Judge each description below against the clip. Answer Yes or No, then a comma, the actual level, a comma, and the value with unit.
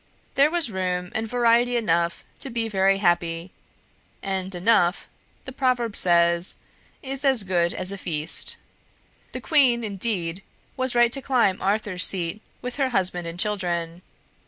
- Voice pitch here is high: Yes, high, 195 Hz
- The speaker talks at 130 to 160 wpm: Yes, average, 145 wpm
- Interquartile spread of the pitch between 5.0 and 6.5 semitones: Yes, average, 5.3 semitones